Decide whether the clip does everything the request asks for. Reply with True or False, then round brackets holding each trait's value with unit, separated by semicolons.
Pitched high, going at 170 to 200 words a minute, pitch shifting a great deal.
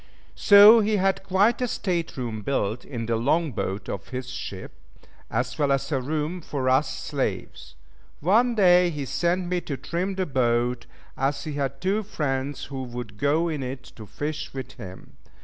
False (145 Hz; 180 wpm; 6.0 semitones)